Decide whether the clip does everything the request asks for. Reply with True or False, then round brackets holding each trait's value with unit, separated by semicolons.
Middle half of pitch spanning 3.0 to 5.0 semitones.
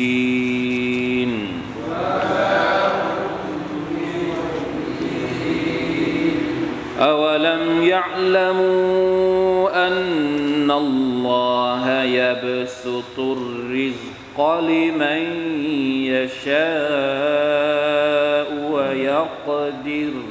True (4.3 semitones)